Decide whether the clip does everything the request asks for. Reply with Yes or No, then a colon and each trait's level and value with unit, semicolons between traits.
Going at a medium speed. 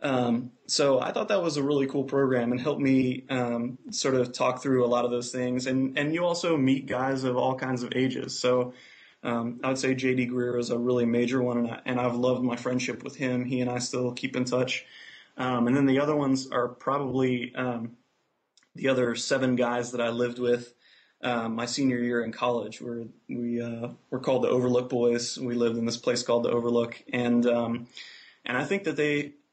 No: fast, 220 wpm